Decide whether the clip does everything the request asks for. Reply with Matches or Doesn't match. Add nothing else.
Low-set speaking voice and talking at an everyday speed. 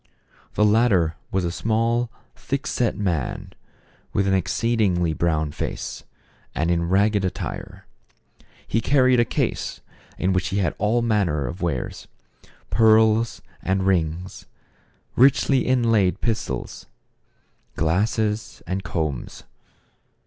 Doesn't match